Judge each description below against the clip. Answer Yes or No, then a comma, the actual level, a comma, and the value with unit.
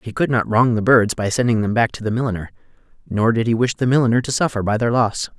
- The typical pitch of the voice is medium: No, low, 115 Hz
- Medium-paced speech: No, fast, 265 wpm